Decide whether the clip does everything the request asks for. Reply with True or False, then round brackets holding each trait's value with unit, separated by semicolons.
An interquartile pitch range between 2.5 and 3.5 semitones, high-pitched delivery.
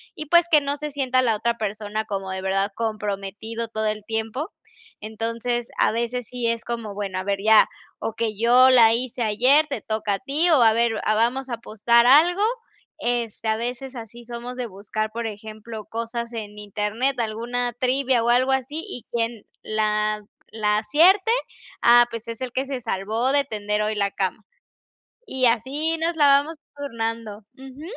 True (3.1 semitones; 230 Hz)